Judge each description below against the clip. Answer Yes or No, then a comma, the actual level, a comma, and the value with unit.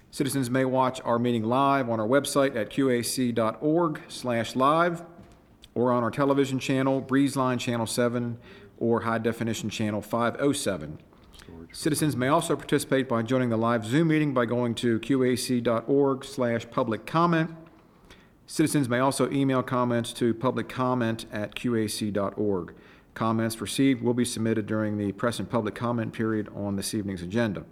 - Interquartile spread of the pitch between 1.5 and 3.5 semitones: Yes, average, 3.2 semitones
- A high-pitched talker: No, low, 120 Hz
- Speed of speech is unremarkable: Yes, average, 145 wpm